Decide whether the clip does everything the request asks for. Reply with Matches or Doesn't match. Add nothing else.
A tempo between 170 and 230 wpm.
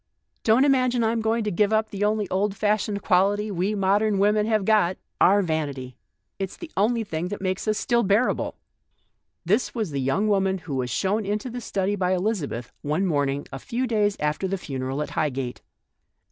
Matches